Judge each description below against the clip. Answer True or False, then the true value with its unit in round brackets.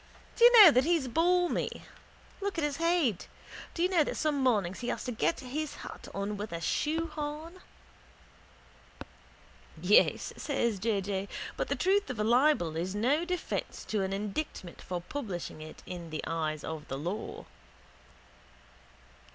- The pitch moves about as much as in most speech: False (8.9 semitones)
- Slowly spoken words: False (160 wpm)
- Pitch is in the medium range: False (245 Hz)